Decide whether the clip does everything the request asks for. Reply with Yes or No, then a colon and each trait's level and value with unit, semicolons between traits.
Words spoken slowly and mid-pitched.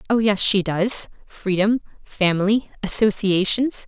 No: slow, 110 wpm; high, 205 Hz